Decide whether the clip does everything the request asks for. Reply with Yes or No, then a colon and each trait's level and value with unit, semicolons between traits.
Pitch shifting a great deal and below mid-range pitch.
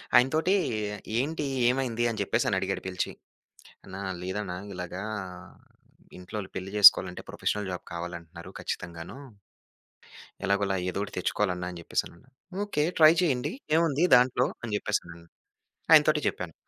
Yes: wide, 6.3 semitones; low, 100 Hz